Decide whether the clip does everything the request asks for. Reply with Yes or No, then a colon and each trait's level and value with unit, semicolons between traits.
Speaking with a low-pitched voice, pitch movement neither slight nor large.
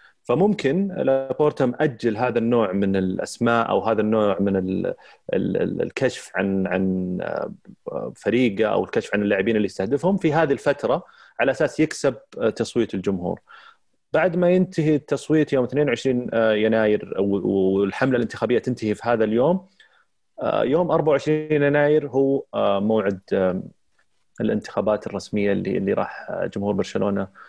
No: low, 115 Hz; wide, 6.7 semitones